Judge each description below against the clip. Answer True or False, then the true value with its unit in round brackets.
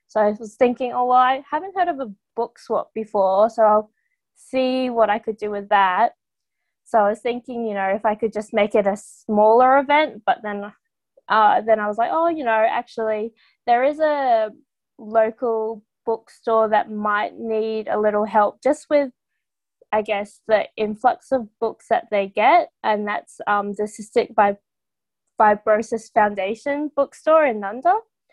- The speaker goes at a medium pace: True (170 wpm)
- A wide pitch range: False (3.4 semitones)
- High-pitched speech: True (220 Hz)